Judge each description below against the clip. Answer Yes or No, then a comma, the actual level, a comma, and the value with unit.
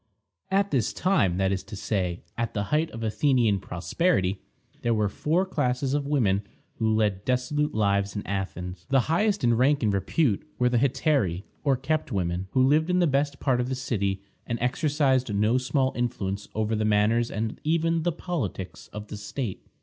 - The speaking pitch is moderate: No, low, 120 Hz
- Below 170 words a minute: No, average, 190 wpm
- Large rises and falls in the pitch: Yes, wide, 6.1 semitones